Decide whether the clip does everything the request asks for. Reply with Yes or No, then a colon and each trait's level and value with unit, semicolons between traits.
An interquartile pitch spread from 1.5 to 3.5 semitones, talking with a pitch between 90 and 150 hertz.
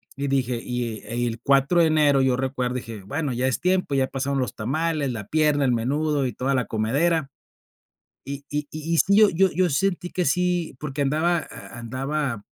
No: average, 3.9 semitones; medium, 140 Hz